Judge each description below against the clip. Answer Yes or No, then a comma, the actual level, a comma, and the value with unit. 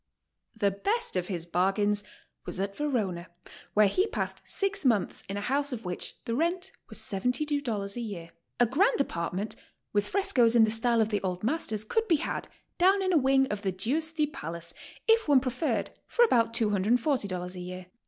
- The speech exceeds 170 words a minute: Yes, average, 185 wpm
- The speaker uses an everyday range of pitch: No, wide, 7.0 semitones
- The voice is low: No, high, 225 Hz